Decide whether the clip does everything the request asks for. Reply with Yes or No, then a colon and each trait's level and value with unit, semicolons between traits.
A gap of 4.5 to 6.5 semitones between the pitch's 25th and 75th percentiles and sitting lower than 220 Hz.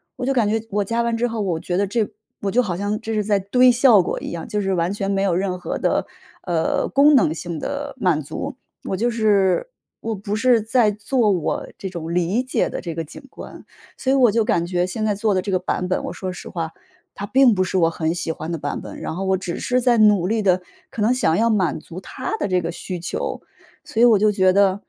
No: average, 4.1 semitones; high, 200 Hz